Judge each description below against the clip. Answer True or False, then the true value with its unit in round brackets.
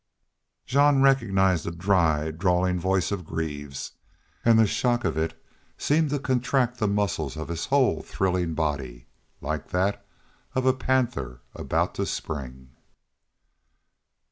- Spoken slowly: True (130 wpm)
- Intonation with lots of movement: True (7.8 semitones)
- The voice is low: True (90 Hz)